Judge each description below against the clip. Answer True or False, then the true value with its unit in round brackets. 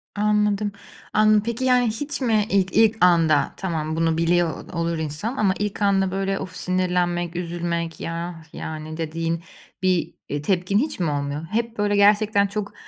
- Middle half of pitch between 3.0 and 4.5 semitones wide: True (3.9 semitones)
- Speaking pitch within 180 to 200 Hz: True (185 Hz)